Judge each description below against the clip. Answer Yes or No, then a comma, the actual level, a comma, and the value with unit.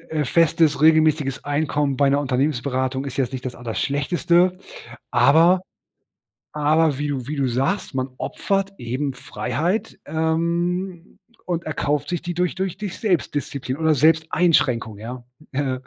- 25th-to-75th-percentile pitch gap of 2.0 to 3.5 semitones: No, average, 4.2 semitones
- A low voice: No, medium, 150 Hz